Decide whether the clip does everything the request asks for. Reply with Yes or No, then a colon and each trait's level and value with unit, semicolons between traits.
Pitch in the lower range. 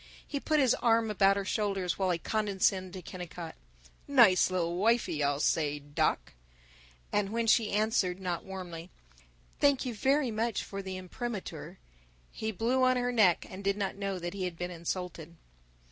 No: high, 195 Hz